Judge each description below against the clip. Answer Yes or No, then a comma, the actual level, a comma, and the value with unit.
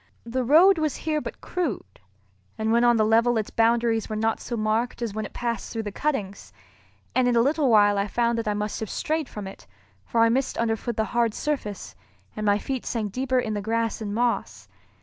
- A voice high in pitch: Yes, high, 230 Hz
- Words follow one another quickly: Yes, fast, 220 wpm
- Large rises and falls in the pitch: No, narrow, 2.5 semitones